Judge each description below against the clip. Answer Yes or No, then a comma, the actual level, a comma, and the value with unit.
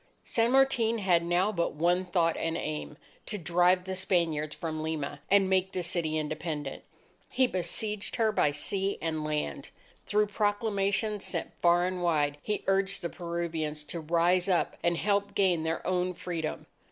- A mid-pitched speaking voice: Yes, medium, 175 Hz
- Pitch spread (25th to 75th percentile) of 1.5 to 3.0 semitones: No, average, 3.4 semitones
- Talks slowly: No, average, 165 wpm